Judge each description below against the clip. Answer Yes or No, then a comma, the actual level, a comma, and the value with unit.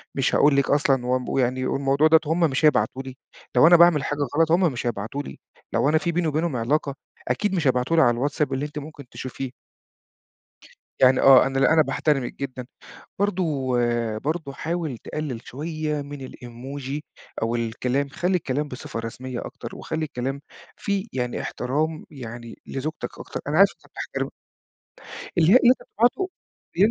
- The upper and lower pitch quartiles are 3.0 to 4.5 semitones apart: Yes, average, 3.6 semitones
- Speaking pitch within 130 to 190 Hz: Yes, medium, 140 Hz